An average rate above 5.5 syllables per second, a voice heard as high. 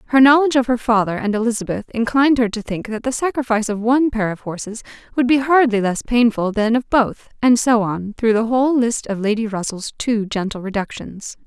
Yes: 5.7 syllables/s; high, 230 Hz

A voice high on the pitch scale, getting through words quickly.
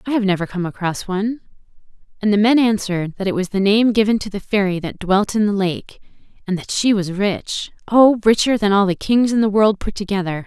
Yes: high, 200 Hz; fast, 225 wpm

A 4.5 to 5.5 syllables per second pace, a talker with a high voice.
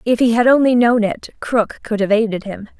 Yes: 5.2 syllables/s; high, 225 Hz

